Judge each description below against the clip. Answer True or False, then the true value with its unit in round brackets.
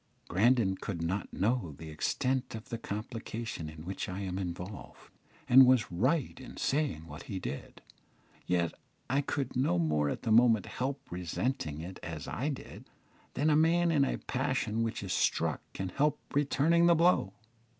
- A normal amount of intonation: False (7.3 semitones)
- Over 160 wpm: True (170 wpm)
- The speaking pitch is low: True (110 Hz)